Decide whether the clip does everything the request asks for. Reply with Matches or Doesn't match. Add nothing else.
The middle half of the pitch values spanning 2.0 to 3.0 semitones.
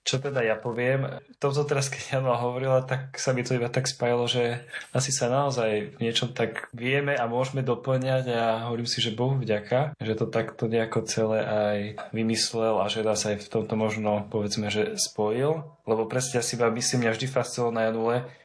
Matches